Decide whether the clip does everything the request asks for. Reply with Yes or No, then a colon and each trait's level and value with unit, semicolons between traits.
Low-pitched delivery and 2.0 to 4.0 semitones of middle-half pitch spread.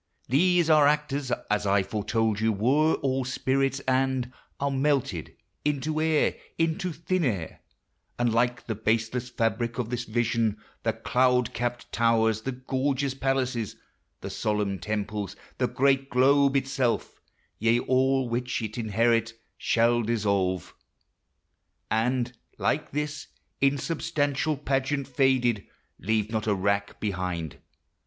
Yes: low, 125 Hz; average, 3.6 semitones